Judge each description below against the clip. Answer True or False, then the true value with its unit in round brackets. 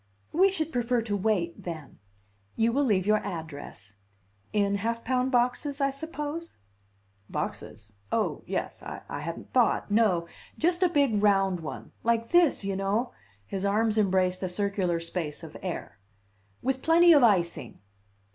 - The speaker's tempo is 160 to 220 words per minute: False (145 wpm)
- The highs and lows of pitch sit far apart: True (6.2 semitones)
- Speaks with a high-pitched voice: True (210 Hz)